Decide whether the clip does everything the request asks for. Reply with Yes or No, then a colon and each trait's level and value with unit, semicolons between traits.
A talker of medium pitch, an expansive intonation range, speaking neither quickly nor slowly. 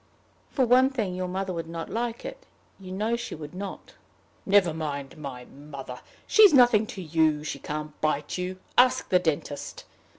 Yes: medium, 180 Hz; wide, 7.0 semitones; average, 170 wpm